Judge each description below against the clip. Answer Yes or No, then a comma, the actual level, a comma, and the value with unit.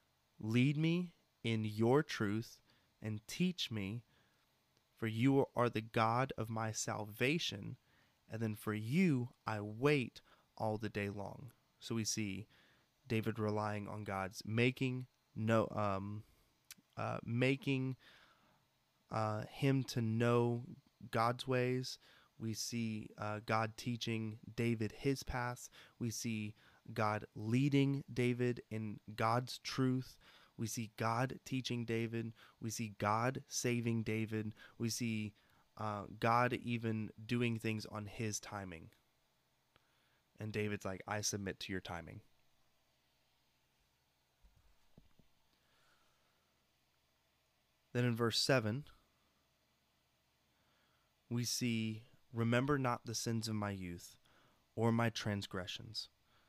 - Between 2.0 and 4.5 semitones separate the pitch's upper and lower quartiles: Yes, average, 2.7 semitones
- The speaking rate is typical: No, slow, 110 wpm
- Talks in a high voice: No, low, 110 Hz